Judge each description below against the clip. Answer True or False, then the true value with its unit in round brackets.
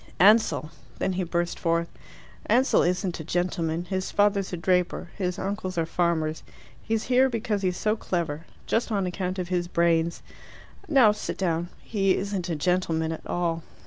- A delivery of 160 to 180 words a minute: True (165 wpm)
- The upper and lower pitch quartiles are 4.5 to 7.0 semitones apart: False (3.0 semitones)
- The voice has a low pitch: False (180 Hz)